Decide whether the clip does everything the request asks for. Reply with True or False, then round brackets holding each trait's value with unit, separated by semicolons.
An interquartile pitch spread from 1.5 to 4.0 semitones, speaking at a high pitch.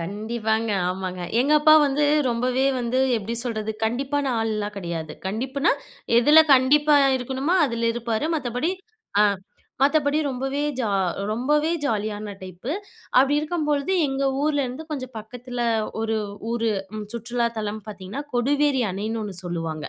False (4.5 semitones; 240 Hz)